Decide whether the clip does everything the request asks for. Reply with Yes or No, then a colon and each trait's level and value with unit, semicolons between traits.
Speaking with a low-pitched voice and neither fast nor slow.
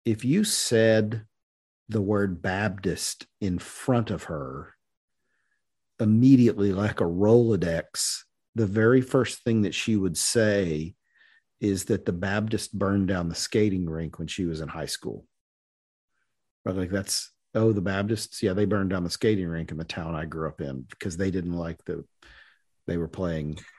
Yes: low, 100 Hz; average, 160 wpm